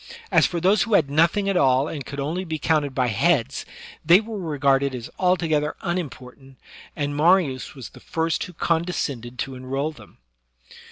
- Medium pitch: Yes, medium, 150 Hz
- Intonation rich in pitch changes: No, average, 4.3 semitones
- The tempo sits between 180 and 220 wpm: No, average, 170 wpm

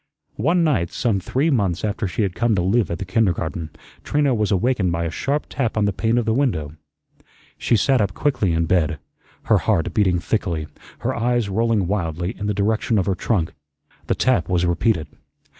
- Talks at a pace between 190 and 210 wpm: Yes, average, 195 wpm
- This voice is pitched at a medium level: No, low, 100 Hz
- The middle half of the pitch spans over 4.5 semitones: Yes, average, 5.0 semitones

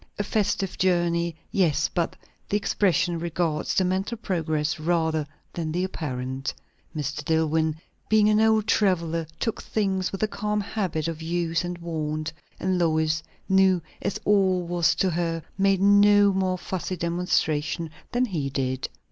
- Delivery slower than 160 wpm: Yes, average, 150 wpm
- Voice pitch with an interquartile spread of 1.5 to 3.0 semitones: No, average, 3.5 semitones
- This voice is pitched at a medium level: Yes, medium, 175 Hz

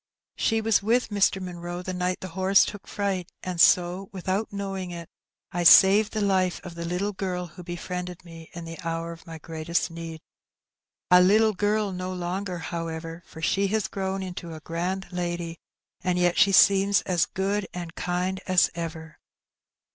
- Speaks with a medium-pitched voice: Yes, medium, 180 Hz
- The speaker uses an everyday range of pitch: No, narrow, 2.3 semitones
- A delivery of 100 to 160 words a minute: No, average, 175 wpm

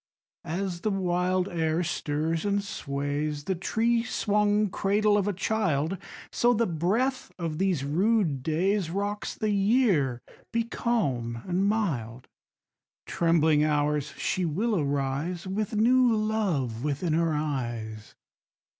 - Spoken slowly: Yes, slow, 130 wpm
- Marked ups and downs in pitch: Yes, wide, 5.8 semitones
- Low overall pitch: No, medium, 175 Hz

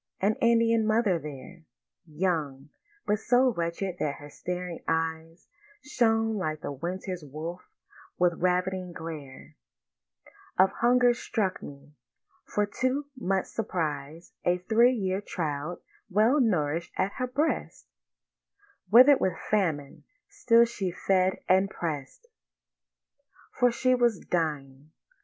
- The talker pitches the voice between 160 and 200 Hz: Yes, medium, 185 Hz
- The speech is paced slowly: Yes, slow, 115 wpm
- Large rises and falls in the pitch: Yes, wide, 5.7 semitones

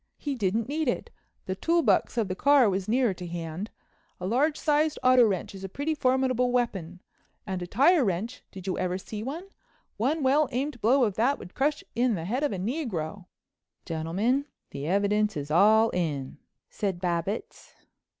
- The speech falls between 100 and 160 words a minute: No, average, 180 wpm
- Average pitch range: No, wide, 6.3 semitones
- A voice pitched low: No, high, 215 Hz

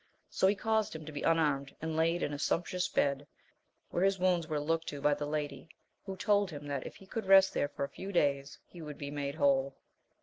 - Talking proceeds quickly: Yes, fast, 235 wpm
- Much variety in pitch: No, average, 4.1 semitones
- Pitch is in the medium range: Yes, medium, 155 Hz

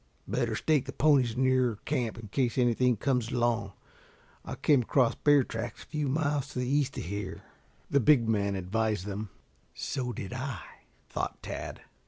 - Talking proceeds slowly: No, average, 170 wpm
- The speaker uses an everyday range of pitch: Yes, average, 3.5 semitones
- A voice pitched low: Yes, low, 125 Hz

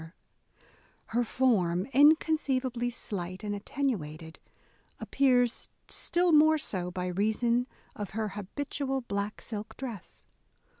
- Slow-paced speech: Yes, slow, 100 wpm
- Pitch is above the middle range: Yes, high, 235 Hz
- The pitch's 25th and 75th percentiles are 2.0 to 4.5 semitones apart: No, wide, 5.4 semitones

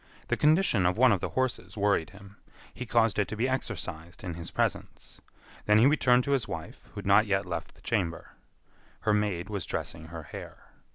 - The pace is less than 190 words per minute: No, fast, 205 wpm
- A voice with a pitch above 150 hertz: No, low, 105 Hz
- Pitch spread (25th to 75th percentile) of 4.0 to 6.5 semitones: Yes, average, 5.3 semitones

